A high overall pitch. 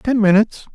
Yes: high, 215 Hz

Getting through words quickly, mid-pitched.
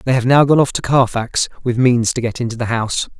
No: fast, 265 wpm; low, 125 Hz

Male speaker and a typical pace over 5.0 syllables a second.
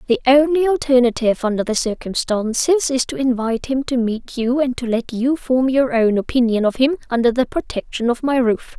No: female; 5.4 syllables/s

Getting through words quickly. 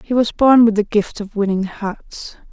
Yes: fast, 215 wpm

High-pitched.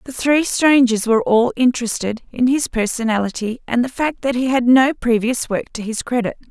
Yes: high, 245 Hz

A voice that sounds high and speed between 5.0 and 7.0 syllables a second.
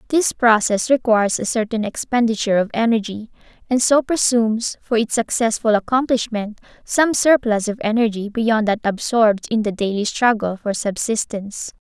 Yes: high, 225 Hz; 5.1 syllables/s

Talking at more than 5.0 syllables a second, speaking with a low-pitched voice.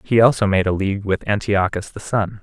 Yes: 5.6 syllables/s; low, 100 Hz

